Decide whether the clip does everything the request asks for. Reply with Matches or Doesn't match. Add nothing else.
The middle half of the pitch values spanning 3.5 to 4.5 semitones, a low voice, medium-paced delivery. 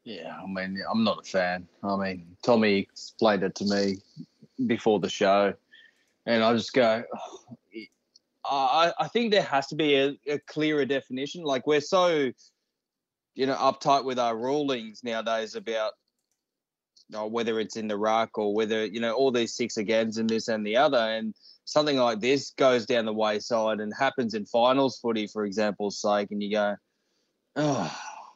Matches